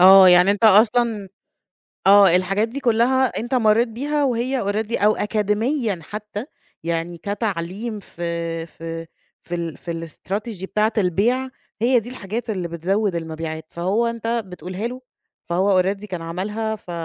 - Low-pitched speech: No, high, 205 Hz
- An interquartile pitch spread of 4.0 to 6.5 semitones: Yes, average, 4.4 semitones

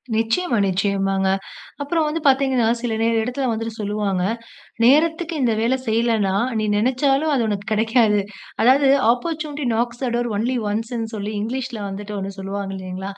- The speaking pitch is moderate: No, high, 230 Hz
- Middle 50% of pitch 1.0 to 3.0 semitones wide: No, average, 4.3 semitones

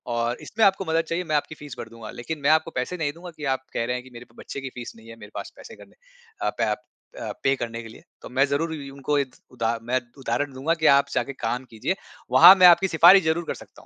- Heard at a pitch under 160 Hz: Yes, medium, 140 Hz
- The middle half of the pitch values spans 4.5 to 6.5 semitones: Yes, average, 5.1 semitones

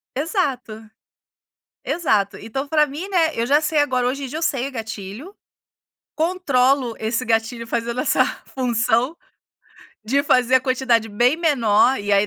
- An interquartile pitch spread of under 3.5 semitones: No, average, 4.3 semitones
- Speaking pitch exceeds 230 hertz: Yes, very high, 255 Hz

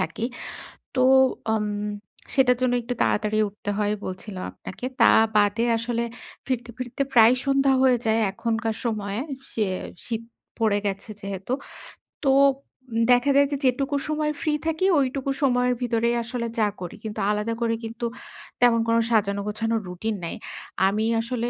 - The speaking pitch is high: Yes, high, 230 Hz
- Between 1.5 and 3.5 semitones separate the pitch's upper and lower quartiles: Yes, average, 2.9 semitones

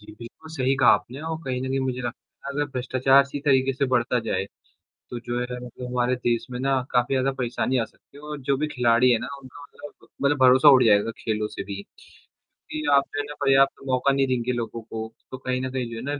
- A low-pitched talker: Yes, low, 130 Hz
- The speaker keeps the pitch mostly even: Yes, narrow, 2.2 semitones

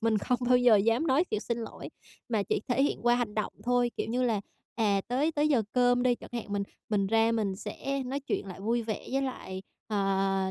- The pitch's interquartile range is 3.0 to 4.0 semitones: Yes, average, 3.3 semitones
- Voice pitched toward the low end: No, high, 230 Hz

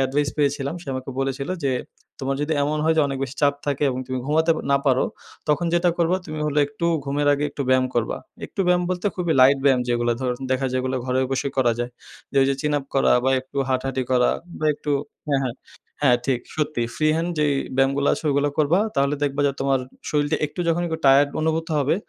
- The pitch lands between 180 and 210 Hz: No, medium, 140 Hz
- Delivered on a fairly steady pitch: Yes, narrow, 2.3 semitones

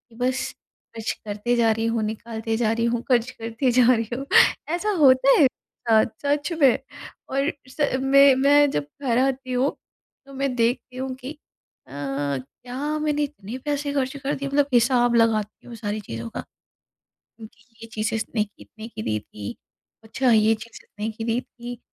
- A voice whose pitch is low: No, high, 240 Hz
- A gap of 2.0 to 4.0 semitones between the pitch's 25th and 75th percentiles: Yes, average, 3.3 semitones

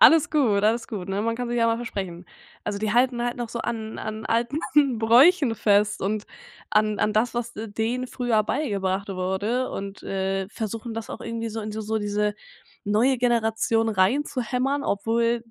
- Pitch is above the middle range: Yes, high, 225 Hz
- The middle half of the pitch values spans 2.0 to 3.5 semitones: Yes, narrow, 2.5 semitones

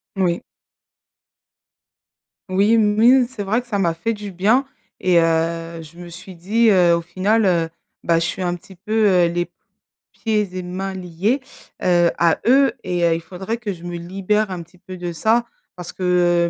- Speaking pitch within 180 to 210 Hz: Yes, medium, 185 Hz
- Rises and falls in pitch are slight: No, average, 3.5 semitones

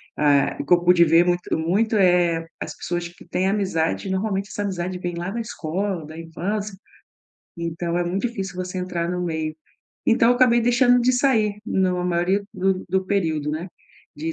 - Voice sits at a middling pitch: Yes, medium, 180 Hz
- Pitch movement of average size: Yes, average, 3.1 semitones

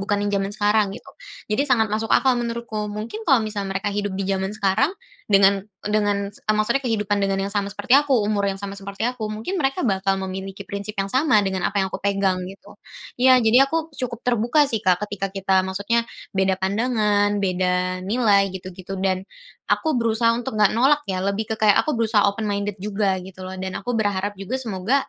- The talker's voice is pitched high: Yes, high, 205 Hz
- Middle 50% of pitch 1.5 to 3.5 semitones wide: Yes, average, 2.8 semitones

